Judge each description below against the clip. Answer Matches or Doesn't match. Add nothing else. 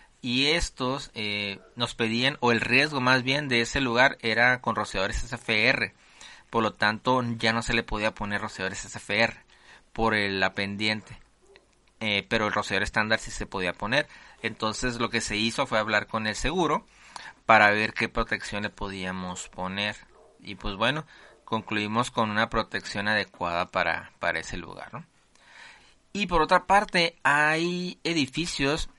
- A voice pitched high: Doesn't match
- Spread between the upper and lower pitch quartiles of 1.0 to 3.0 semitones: Doesn't match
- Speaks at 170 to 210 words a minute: Doesn't match